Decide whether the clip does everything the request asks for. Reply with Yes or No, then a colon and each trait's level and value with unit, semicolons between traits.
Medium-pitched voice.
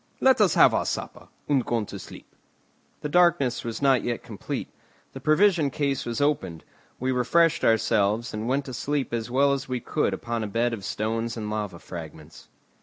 No: low, 120 Hz